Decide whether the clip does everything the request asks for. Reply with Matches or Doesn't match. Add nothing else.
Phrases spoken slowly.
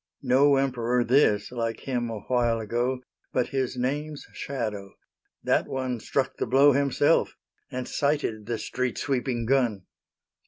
Matches